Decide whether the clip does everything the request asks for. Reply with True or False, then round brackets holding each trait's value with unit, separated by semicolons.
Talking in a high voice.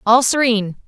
True (230 Hz)